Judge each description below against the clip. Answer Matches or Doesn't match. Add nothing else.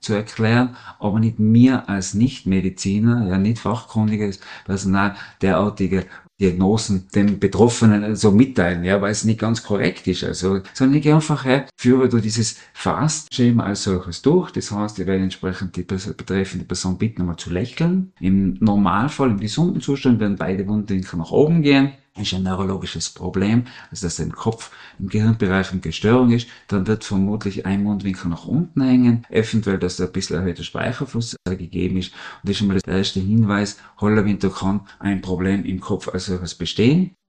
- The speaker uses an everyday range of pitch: Matches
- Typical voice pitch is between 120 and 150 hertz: Doesn't match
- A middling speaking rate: Matches